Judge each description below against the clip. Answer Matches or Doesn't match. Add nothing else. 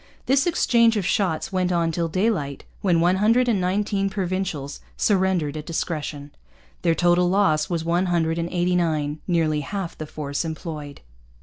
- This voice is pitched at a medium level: Matches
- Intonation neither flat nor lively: Matches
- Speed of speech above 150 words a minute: Matches